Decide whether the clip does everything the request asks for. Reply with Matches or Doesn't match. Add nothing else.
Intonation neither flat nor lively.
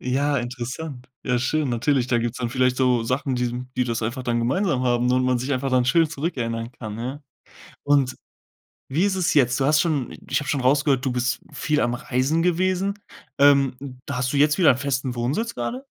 Matches